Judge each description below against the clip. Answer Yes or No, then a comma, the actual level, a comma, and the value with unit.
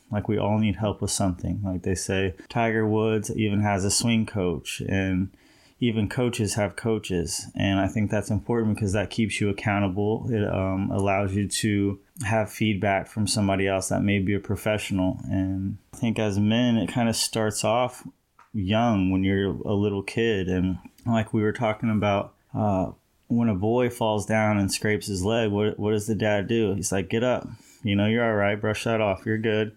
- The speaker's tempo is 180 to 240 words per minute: Yes, average, 200 wpm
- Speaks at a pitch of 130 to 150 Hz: No, low, 105 Hz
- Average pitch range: No, narrow, 2.2 semitones